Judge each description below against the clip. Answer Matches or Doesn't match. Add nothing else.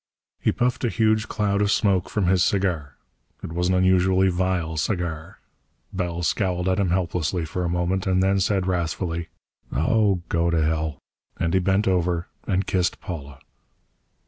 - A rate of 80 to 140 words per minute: Doesn't match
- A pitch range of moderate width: Doesn't match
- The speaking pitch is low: Matches